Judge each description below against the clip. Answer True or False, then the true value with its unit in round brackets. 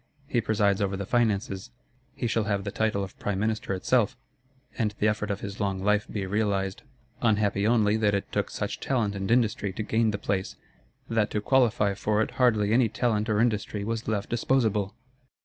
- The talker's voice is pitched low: True (105 Hz)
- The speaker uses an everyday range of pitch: False (2.0 semitones)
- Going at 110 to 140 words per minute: False (190 wpm)